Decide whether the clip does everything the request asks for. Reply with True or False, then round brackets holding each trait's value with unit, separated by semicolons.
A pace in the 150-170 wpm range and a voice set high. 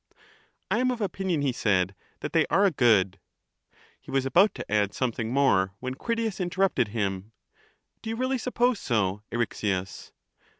False (165 wpm; 130 Hz)